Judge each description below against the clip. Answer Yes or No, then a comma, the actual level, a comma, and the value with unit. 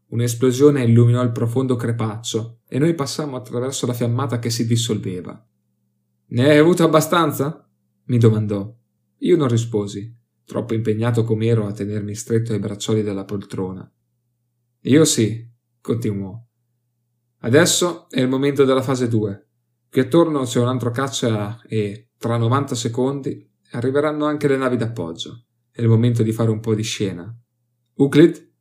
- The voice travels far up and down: No, average, 3.0 semitones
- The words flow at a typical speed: Yes, average, 145 wpm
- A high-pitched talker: No, low, 120 Hz